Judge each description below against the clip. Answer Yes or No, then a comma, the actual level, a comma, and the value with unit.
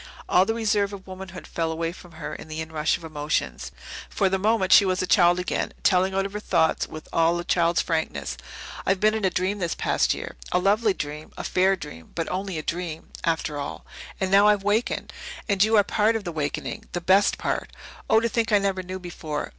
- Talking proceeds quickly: Yes, fast, 220 wpm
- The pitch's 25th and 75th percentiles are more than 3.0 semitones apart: Yes, average, 3.4 semitones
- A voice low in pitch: No, medium, 185 Hz